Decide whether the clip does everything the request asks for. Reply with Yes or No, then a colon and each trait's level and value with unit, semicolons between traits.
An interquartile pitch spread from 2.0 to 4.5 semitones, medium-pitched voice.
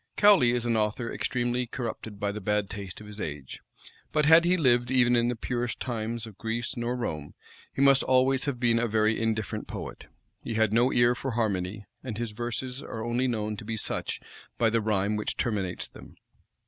No: narrow, 2.5 semitones; low, 115 Hz